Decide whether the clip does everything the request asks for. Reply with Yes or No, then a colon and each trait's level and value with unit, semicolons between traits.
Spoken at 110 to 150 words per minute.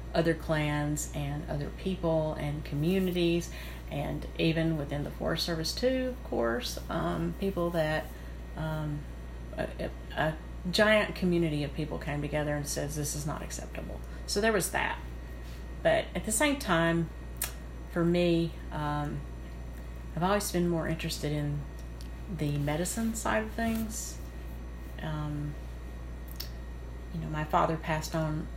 Yes: slow, 135 wpm